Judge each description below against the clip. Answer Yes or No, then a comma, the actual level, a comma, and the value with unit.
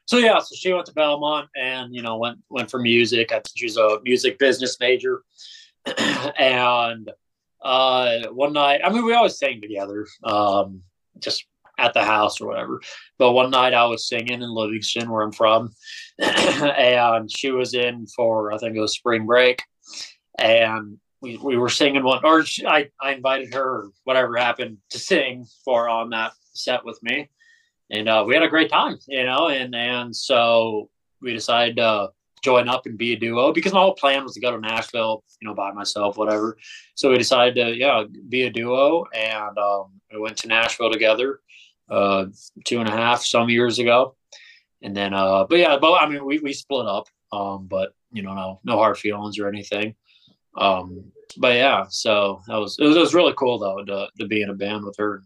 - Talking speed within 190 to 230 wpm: Yes, average, 200 wpm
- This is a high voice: No, low, 120 Hz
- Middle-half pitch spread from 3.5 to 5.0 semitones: Yes, average, 3.8 semitones